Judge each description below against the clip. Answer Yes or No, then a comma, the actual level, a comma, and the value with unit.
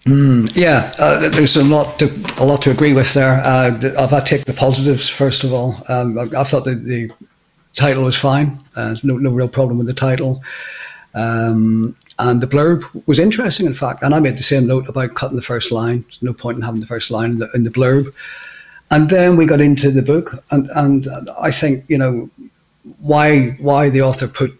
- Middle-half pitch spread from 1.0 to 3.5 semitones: Yes, average, 2.7 semitones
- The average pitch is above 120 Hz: Yes, low, 135 Hz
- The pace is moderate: No, fast, 220 wpm